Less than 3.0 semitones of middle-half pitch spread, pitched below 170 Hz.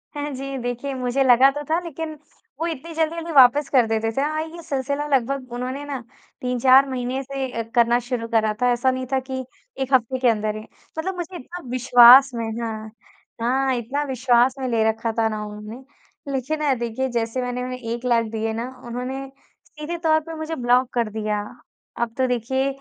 No: narrow, 2.6 semitones; very high, 255 Hz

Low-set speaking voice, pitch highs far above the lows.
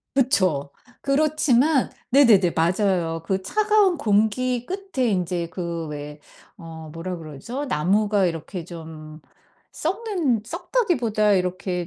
No: high, 200 Hz; wide, 7.9 semitones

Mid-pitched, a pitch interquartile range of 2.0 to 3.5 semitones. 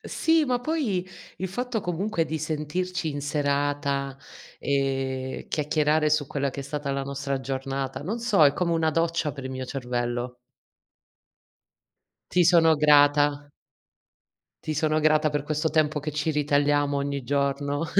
Yes: medium, 145 Hz; narrow, 2.4 semitones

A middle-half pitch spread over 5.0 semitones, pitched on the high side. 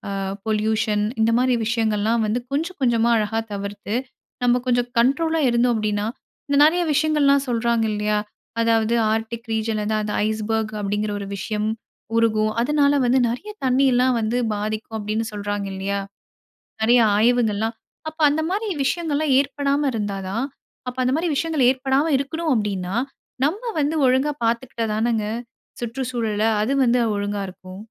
No: average, 3.9 semitones; high, 230 Hz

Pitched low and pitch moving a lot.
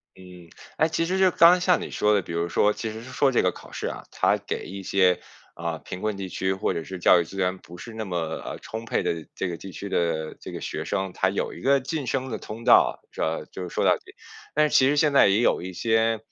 Yes: low, 100 Hz; wide, 6.1 semitones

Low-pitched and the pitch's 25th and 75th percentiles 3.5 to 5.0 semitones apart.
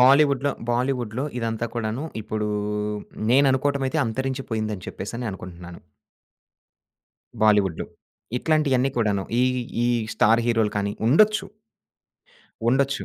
Yes: low, 120 Hz; average, 4.1 semitones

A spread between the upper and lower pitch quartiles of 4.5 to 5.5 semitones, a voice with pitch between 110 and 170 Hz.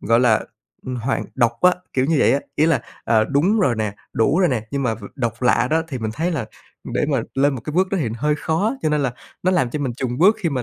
Yes: average, 5.1 semitones; low, 135 Hz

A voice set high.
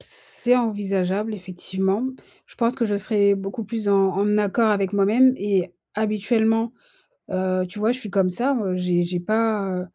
Yes: high, 205 Hz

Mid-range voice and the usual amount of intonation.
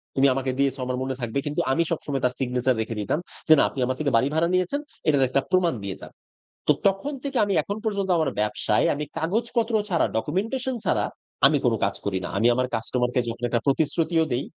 No: medium, 145 Hz; wide, 6.5 semitones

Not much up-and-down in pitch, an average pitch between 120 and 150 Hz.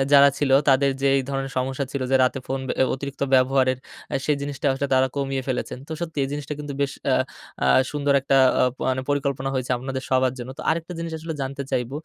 Yes: narrow, 1.5 semitones; low, 135 Hz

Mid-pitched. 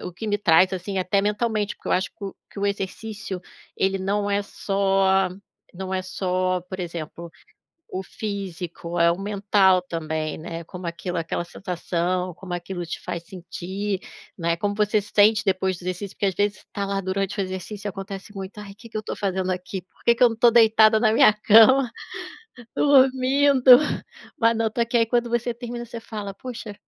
No: high, 195 Hz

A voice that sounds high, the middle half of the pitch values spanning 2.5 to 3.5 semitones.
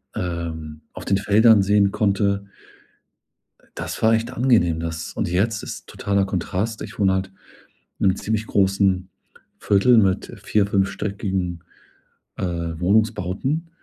No: low, 100 Hz; average, 2.8 semitones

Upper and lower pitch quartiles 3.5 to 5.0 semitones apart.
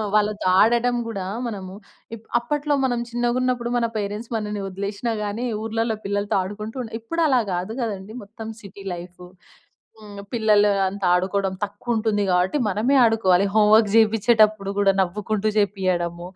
No: narrow, 2.5 semitones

